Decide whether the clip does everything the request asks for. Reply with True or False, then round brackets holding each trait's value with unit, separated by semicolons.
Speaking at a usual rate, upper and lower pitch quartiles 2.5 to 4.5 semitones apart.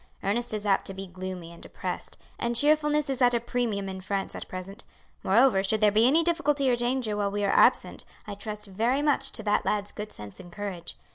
False (220 wpm; 4.2 semitones)